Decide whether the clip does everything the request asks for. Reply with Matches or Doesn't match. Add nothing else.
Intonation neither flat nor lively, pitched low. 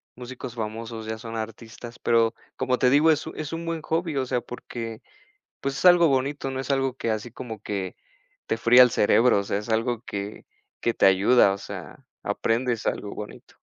Matches